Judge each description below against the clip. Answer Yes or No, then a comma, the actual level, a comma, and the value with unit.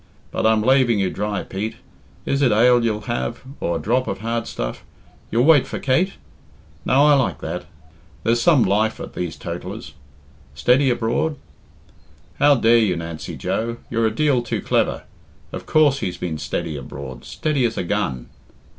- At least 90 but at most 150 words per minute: No, average, 170 wpm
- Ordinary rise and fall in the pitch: Yes, average, 4.9 semitones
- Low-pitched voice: Yes, low, 115 Hz